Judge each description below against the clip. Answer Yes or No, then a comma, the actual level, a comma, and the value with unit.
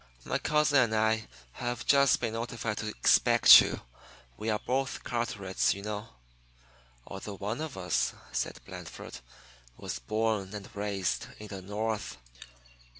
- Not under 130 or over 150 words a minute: Yes, average, 140 wpm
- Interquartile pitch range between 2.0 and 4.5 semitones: Yes, average, 2.9 semitones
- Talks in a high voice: No, low, 110 Hz